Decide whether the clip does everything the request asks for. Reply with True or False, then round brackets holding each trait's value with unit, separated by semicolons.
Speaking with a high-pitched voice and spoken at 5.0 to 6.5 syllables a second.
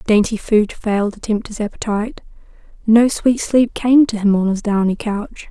False (215 Hz; 4.8 syllables/s)